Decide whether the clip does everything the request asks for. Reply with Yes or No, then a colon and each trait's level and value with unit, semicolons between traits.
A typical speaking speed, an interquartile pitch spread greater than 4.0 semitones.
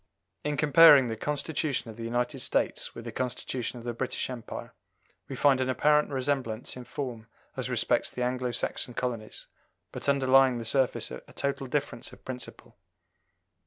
No: average, 160 wpm; narrow, 2.5 semitones